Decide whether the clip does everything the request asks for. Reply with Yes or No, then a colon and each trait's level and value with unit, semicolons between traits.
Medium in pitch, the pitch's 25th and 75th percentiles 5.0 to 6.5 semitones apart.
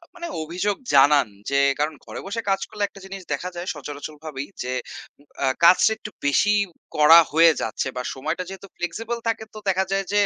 Yes: medium, 180 Hz; wide, 5.4 semitones